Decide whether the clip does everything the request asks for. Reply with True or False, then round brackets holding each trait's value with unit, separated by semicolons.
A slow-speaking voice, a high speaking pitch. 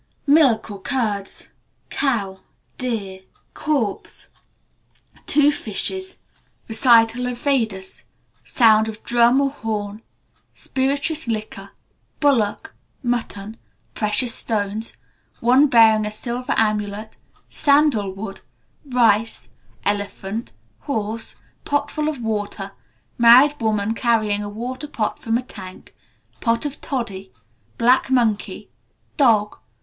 True (100 wpm; 225 Hz)